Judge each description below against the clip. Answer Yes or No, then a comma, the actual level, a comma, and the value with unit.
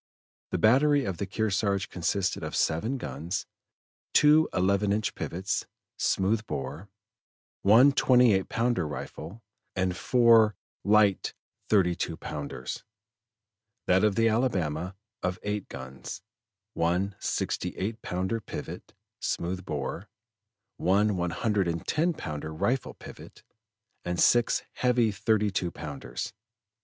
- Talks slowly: Yes, slow, 120 wpm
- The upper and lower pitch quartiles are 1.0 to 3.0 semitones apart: No, average, 4.4 semitones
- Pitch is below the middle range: Yes, low, 100 Hz